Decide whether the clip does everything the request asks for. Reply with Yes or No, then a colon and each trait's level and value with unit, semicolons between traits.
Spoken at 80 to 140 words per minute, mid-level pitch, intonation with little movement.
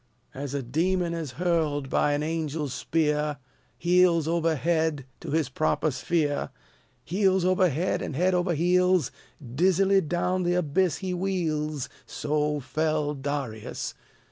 No: slow, 135 wpm; medium, 160 Hz; average, 3.4 semitones